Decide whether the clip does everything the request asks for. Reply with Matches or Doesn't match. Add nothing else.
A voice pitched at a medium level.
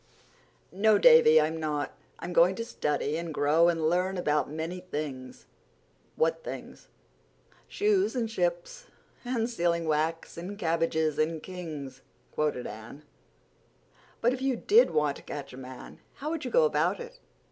Matches